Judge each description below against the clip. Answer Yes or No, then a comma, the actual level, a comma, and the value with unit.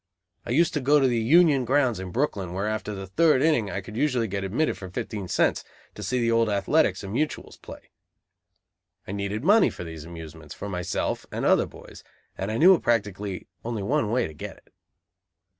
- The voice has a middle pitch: No, low, 110 Hz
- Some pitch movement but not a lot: No, wide, 5.9 semitones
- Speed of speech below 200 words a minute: No, fast, 205 wpm